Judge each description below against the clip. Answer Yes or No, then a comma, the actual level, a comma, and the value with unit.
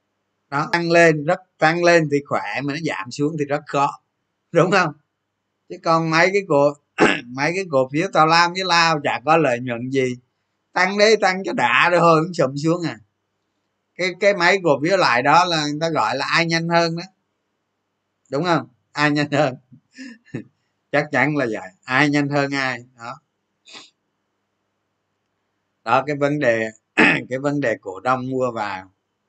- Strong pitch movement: Yes, wide, 7.2 semitones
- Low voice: No, medium, 145 Hz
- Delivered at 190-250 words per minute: No, average, 175 wpm